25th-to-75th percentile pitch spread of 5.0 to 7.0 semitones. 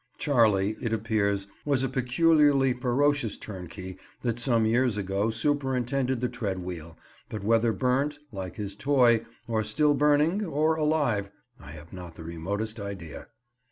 Yes: wide, 5.4 semitones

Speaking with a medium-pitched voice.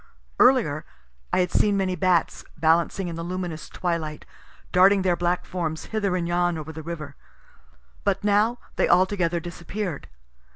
Yes: medium, 175 Hz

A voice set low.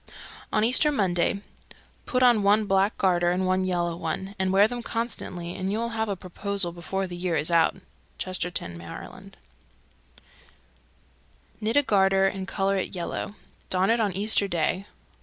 No: high, 190 Hz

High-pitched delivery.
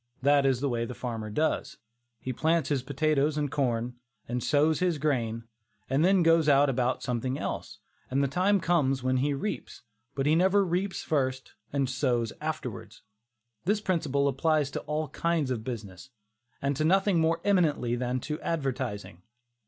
No: medium, 140 Hz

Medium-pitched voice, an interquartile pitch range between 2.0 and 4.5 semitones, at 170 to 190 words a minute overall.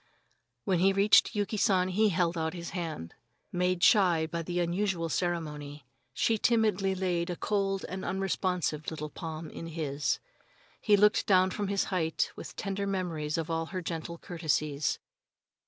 No: medium, 175 Hz; average, 3.1 semitones; average, 155 wpm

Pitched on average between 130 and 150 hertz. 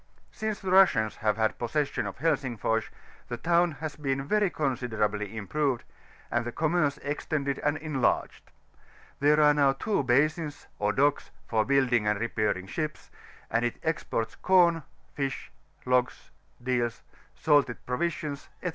Yes: medium, 140 Hz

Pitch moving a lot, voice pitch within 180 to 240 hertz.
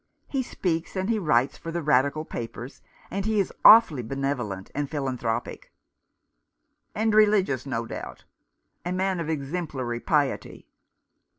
No: wide, 6.4 semitones; medium, 150 Hz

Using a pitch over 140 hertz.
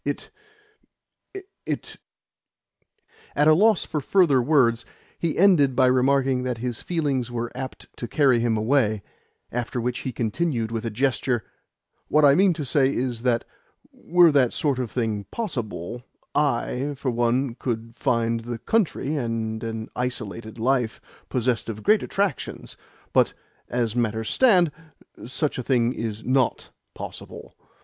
No: low, 125 Hz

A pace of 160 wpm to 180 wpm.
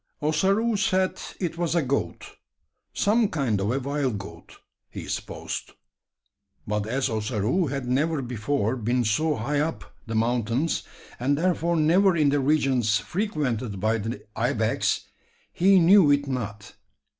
No: average, 140 wpm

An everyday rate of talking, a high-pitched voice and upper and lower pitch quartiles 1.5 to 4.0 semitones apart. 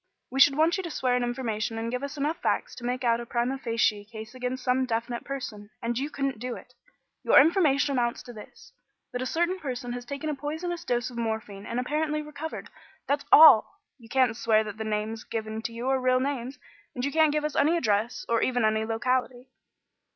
No: fast, 215 wpm; very high, 250 Hz; average, 3.5 semitones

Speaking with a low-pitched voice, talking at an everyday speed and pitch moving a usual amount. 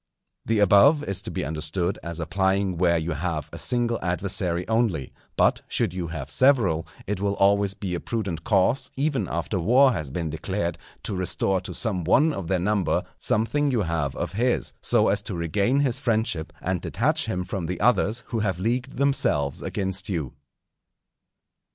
Yes: very low, 95 Hz; average, 175 wpm; average, 4.9 semitones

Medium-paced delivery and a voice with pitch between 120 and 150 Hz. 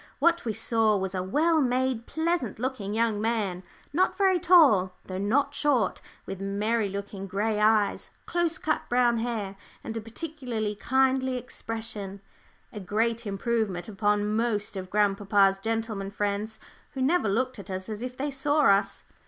No: average, 155 wpm; high, 220 Hz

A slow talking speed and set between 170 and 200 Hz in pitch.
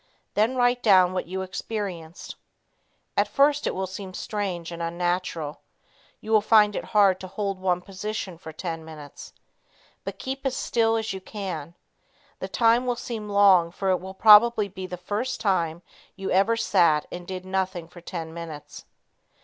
No: average, 170 wpm; high, 190 Hz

